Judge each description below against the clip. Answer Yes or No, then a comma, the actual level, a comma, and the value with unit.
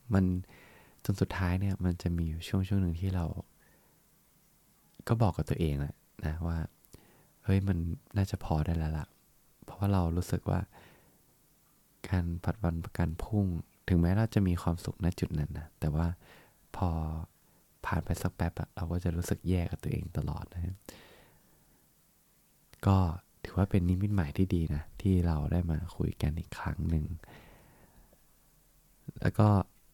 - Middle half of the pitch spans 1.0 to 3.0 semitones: Yes, average, 2.7 semitones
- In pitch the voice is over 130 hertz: No, very low, 90 Hz